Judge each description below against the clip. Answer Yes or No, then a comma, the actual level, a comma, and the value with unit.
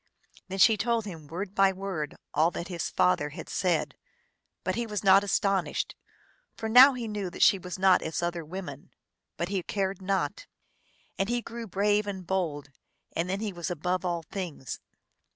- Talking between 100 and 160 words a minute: No, average, 180 wpm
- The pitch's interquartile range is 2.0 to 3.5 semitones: Yes, average, 2.9 semitones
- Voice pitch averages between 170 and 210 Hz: Yes, high, 190 Hz